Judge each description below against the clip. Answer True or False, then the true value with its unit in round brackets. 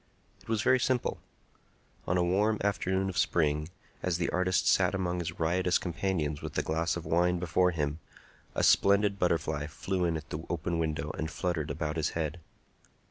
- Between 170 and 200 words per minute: True (180 wpm)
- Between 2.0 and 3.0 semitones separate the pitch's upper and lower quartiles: True (2.7 semitones)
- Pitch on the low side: True (85 Hz)